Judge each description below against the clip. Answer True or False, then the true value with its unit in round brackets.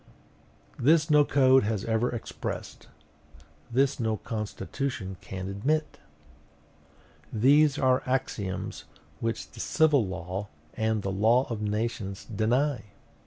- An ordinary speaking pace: False (110 wpm)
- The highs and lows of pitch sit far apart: False (4.4 semitones)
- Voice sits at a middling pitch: False (115 Hz)